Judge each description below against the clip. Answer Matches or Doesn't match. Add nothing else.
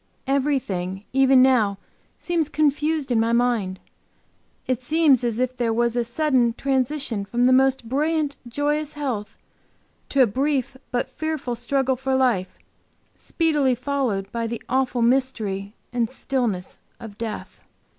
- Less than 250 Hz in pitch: Doesn't match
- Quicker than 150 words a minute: Doesn't match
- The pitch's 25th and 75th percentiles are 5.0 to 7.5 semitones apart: Doesn't match